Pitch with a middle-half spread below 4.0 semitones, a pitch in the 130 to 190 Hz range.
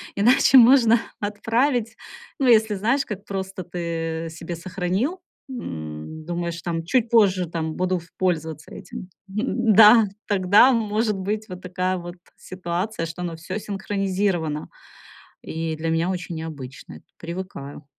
No: average, 4.4 semitones; medium, 185 Hz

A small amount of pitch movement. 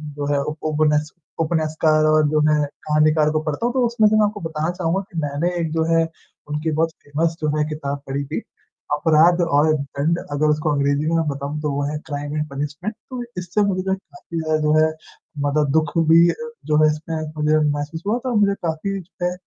Yes: narrow, 2.1 semitones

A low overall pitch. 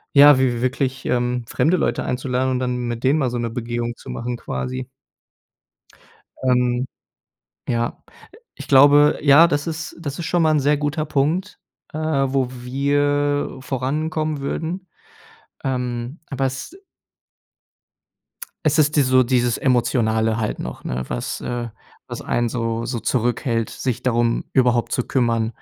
Yes: low, 130 Hz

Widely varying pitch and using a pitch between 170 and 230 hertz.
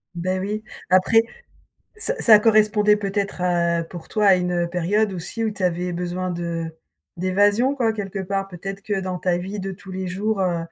No: average, 2.8 semitones; high, 190 Hz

